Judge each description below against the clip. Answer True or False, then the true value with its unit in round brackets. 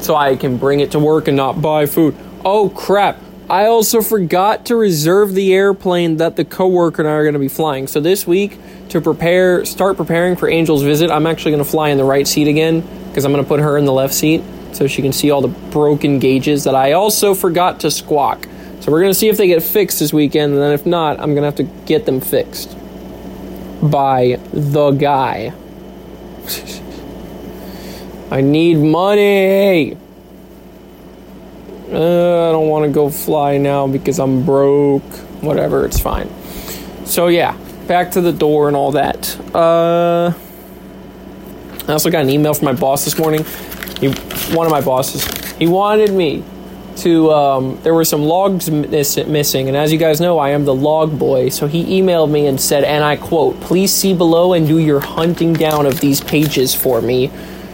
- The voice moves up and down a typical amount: True (3.5 semitones)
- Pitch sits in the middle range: True (155 Hz)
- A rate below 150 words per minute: False (190 wpm)